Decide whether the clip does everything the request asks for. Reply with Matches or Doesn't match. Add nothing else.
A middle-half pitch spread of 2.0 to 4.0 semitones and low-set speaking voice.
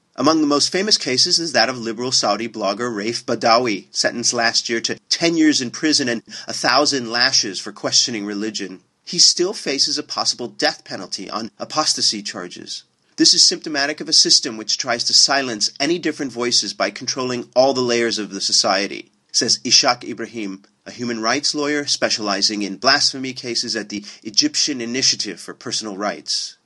Doesn't match